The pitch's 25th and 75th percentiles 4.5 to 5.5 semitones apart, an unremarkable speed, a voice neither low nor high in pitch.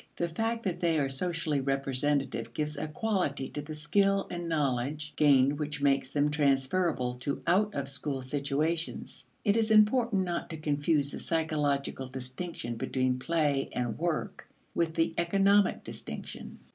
No: average, 3.8 semitones; average, 150 wpm; medium, 150 Hz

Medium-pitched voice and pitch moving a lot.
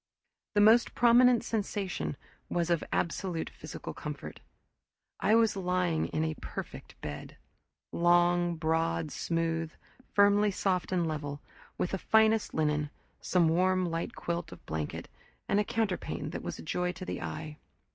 No: medium, 175 Hz; average, 3.8 semitones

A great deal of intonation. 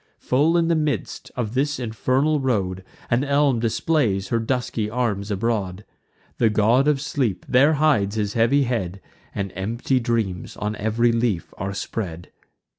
No: average, 4.7 semitones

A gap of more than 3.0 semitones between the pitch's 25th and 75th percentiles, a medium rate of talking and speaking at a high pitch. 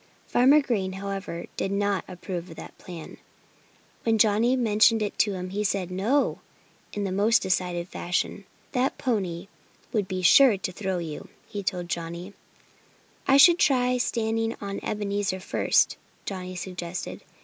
Yes: average, 3.5 semitones; average, 150 wpm; high, 200 Hz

